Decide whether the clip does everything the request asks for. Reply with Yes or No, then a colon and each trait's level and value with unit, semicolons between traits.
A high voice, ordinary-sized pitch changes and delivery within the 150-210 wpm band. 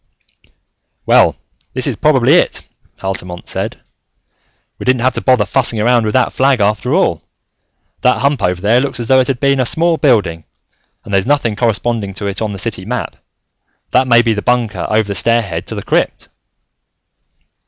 No: low, 115 Hz; average, 3.9 semitones; average, 185 wpm